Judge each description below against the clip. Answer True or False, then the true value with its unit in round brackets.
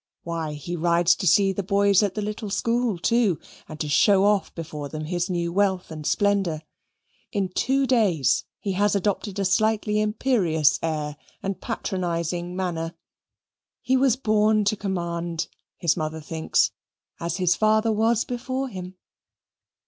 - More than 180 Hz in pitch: True (190 Hz)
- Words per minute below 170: True (150 wpm)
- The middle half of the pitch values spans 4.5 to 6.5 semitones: False (3.9 semitones)